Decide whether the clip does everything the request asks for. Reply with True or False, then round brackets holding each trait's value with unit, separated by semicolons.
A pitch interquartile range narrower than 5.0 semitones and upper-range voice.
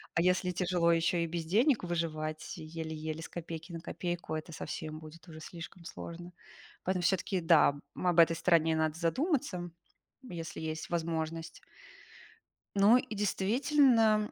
False (2.5 semitones; 170 Hz)